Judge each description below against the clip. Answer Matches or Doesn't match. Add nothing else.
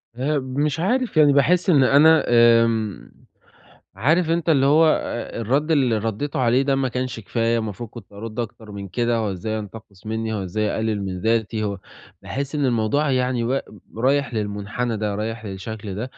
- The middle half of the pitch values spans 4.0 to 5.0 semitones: Matches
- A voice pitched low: Matches